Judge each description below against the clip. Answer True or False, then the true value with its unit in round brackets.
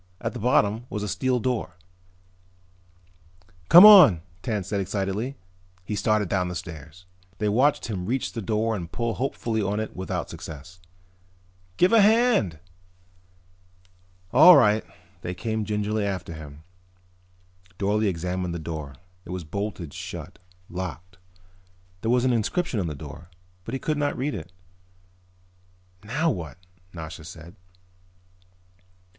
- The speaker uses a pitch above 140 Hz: False (105 Hz)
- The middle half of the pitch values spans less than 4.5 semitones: False (5.1 semitones)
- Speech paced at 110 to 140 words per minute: True (135 wpm)